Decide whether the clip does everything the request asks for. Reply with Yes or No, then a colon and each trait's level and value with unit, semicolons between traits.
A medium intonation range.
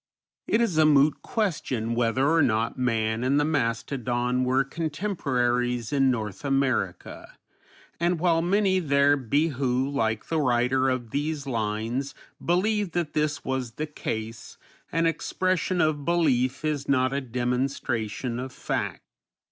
Yes: average, 4.2 semitones